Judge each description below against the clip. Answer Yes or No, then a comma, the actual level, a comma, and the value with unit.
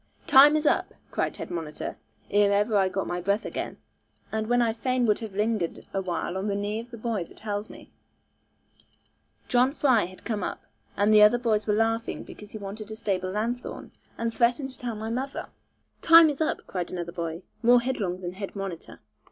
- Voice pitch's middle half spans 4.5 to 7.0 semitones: No, average, 3.5 semitones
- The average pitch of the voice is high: Yes, high, 215 Hz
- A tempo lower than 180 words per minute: No, average, 195 wpm